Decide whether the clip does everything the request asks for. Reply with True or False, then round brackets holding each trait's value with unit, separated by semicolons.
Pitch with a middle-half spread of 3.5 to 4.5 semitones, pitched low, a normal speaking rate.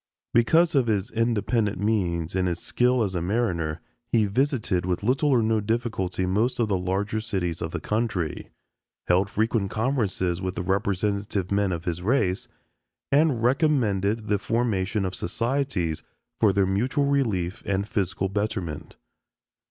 True (4.0 semitones; 105 Hz; 150 wpm)